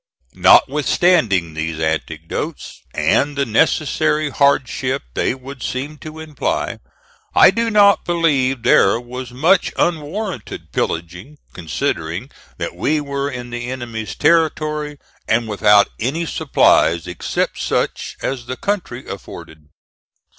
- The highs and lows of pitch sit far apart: Yes, wide, 5.9 semitones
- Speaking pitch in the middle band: No, low, 130 Hz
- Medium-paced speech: No, slow, 115 wpm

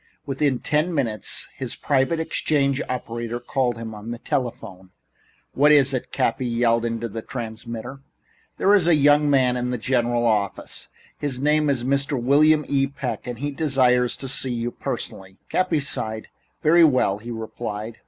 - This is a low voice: Yes, low, 125 Hz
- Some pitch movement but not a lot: Yes, average, 3.5 semitones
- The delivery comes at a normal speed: Yes, average, 165 wpm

